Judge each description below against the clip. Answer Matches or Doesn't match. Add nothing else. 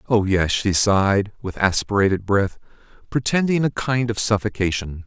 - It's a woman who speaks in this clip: Doesn't match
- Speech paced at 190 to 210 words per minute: Doesn't match